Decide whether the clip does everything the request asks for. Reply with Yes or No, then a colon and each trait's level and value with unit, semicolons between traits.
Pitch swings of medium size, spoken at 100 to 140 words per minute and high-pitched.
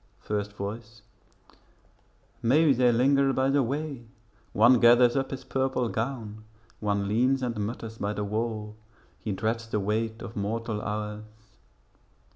No: average, 3.2 semitones; slow, 135 wpm; low, 115 Hz